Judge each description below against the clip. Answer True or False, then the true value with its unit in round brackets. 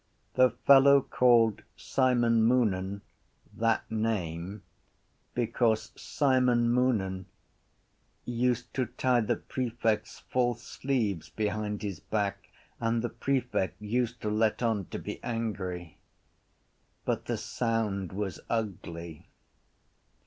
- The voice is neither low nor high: False (115 Hz)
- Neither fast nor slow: False (105 wpm)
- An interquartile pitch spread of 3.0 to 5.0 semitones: True (3.4 semitones)